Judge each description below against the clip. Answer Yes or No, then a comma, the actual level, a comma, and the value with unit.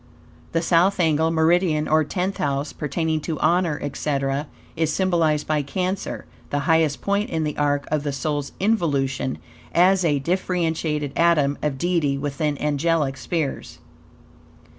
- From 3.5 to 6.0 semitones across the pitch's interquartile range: No, average, 3.0 semitones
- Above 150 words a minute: No, average, 140 wpm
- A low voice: No, medium, 155 Hz